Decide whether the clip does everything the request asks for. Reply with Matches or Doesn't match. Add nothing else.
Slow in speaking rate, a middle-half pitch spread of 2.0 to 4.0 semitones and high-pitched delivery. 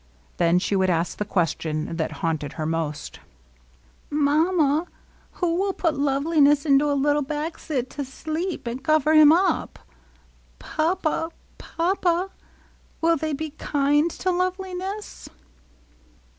Doesn't match